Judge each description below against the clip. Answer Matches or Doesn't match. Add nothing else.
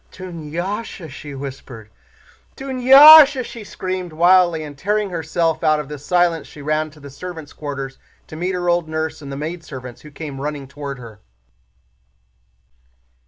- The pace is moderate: Matches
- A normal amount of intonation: Matches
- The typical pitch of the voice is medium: Matches